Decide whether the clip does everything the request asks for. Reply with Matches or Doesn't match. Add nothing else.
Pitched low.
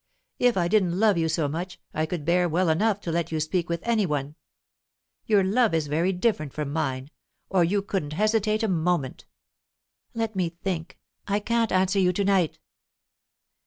Doesn't match